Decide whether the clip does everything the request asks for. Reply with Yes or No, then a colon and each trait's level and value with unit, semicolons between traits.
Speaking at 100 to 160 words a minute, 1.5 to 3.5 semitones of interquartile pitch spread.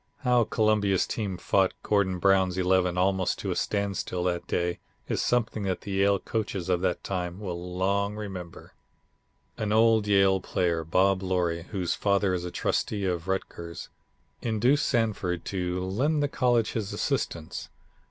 Yes: average, 150 wpm; narrow, 2.6 semitones